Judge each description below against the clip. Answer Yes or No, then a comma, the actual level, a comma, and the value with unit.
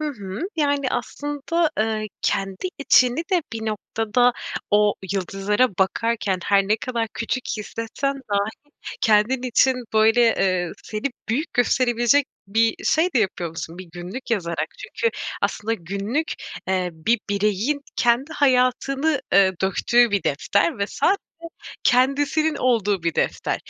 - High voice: Yes, high, 225 Hz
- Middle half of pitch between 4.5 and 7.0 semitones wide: Yes, average, 4.9 semitones